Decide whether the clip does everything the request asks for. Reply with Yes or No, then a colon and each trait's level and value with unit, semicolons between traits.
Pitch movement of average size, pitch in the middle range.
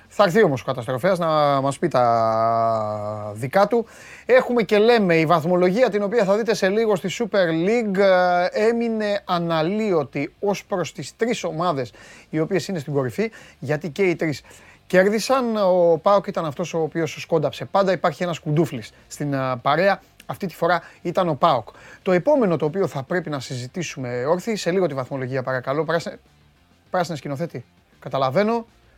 No: wide, 6.2 semitones; medium, 170 Hz